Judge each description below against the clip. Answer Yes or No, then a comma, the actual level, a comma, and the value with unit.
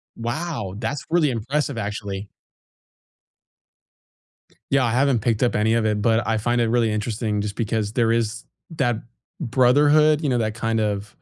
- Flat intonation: No, average, 3.2 semitones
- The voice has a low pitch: Yes, low, 115 Hz